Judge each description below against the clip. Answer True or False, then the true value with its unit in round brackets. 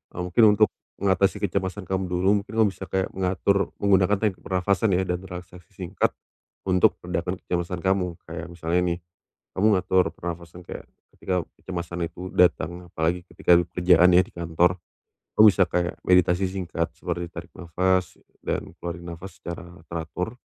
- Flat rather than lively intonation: True (1.6 semitones)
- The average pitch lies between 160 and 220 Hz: False (90 Hz)